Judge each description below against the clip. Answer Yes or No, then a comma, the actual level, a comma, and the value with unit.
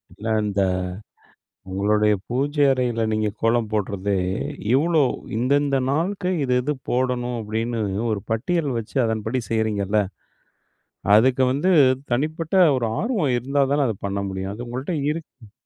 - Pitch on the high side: No, low, 120 Hz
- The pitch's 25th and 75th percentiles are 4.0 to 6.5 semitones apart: Yes, average, 4.8 semitones